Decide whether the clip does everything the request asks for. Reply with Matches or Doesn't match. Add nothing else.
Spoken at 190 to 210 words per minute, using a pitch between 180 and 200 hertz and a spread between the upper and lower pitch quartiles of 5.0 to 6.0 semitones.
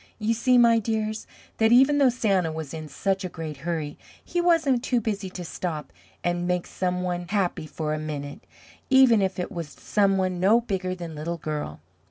Matches